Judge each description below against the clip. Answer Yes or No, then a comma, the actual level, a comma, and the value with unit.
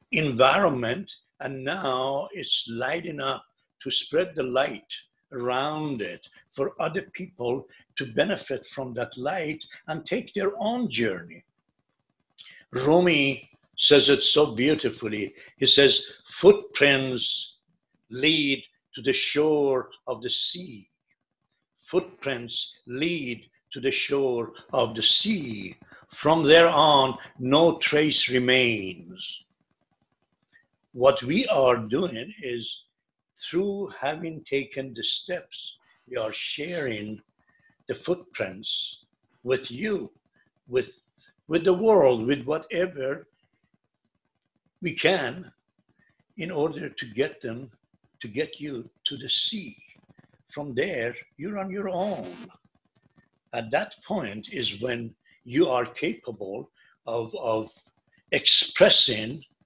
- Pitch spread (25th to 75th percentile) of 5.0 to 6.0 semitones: Yes, average, 5.3 semitones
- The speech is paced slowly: Yes, slow, 110 wpm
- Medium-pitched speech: Yes, medium, 145 Hz